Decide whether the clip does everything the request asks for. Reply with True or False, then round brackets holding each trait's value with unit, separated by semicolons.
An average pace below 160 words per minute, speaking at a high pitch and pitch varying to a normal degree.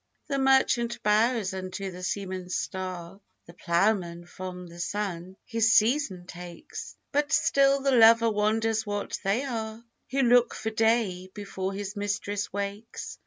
True (140 wpm; 205 Hz; 3.6 semitones)